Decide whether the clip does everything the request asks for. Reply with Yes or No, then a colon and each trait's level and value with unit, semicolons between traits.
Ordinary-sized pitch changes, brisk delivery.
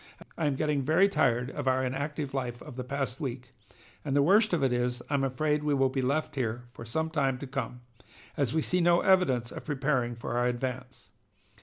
Yes: average, 3.2 semitones; fast, 210 wpm